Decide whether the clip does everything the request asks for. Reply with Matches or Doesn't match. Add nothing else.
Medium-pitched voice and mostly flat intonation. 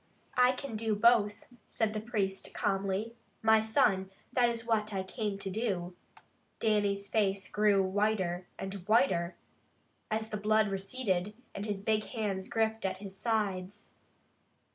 Doesn't match